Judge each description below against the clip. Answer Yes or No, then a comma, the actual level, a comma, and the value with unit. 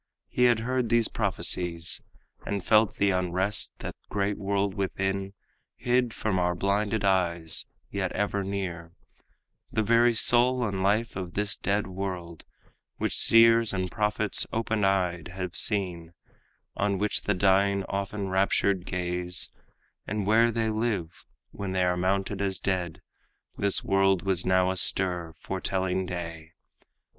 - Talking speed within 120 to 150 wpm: Yes, average, 140 wpm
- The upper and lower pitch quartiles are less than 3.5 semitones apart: Yes, narrow, 2.5 semitones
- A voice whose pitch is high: No, very low, 95 Hz